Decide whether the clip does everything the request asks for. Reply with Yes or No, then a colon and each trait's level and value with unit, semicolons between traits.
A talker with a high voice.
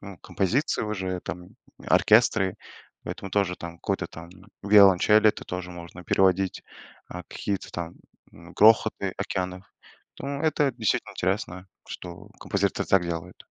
No: very low, 95 Hz